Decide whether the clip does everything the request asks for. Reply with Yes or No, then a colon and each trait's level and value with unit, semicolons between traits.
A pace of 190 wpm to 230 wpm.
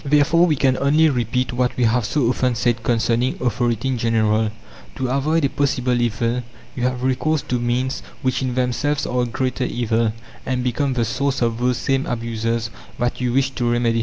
Yes: average, 195 wpm